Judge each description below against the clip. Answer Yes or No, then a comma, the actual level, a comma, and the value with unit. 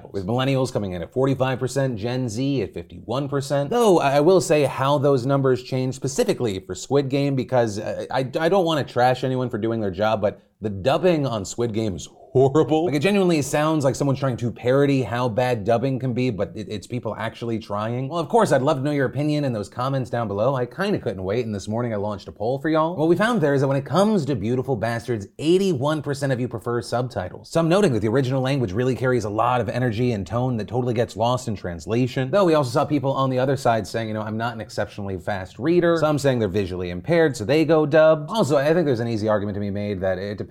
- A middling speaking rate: No, fast, 250 wpm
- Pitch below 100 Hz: No, low, 125 Hz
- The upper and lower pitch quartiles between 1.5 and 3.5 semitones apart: No, average, 4.2 semitones